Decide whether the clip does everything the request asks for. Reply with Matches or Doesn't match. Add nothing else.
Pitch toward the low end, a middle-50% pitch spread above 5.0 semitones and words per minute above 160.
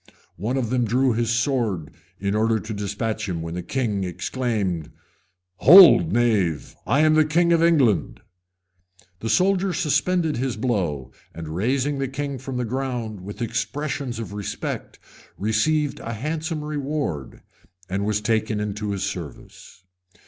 Doesn't match